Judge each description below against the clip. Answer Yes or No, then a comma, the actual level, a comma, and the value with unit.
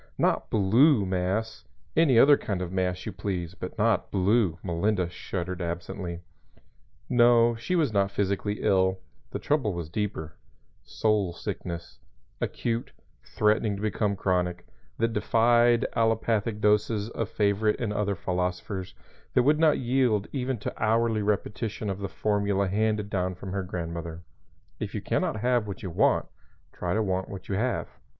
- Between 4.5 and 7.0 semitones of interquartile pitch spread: No, average, 3.5 semitones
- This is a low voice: Yes, low, 100 Hz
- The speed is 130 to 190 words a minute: Yes, average, 155 wpm